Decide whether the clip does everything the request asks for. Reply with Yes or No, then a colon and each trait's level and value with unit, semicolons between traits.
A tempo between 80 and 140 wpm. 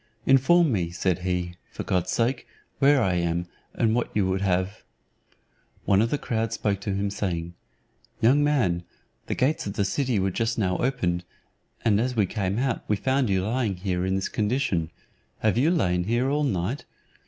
No: average, 185 wpm